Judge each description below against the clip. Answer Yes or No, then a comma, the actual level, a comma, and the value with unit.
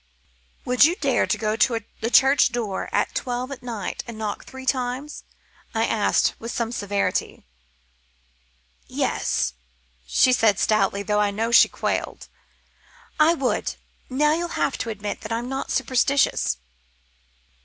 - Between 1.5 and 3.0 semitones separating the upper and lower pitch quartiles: No, average, 3.8 semitones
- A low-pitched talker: No, high, 240 Hz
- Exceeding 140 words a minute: No, slow, 135 wpm